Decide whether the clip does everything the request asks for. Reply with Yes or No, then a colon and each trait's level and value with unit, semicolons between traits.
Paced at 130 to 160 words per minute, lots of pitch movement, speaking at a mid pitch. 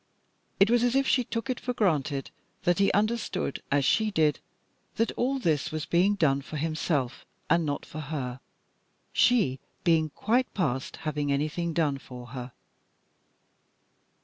Yes: average, 150 wpm; wide, 7.1 semitones; medium, 160 Hz